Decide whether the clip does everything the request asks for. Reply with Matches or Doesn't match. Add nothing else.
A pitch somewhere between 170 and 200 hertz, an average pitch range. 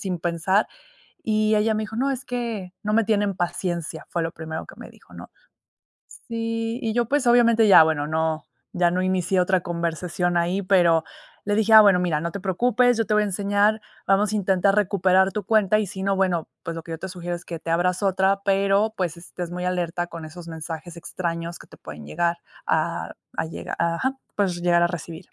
Matches